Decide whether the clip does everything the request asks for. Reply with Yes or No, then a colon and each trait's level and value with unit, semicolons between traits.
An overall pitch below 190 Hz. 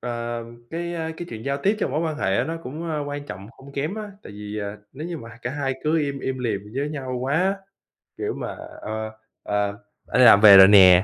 Yes: low, 135 Hz